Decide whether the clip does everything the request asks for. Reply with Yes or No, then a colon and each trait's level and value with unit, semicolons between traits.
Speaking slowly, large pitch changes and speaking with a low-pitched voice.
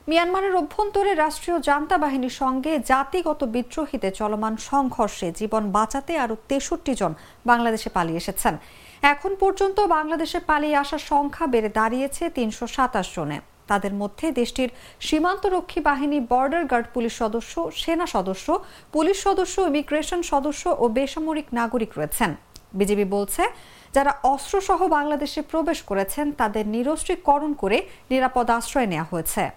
No: slow, 120 wpm; wide, 6.3 semitones; very high, 280 Hz